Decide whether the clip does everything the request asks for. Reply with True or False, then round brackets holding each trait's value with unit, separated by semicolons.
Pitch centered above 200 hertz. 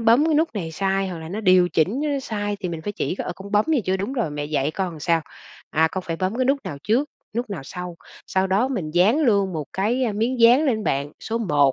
False (195 Hz)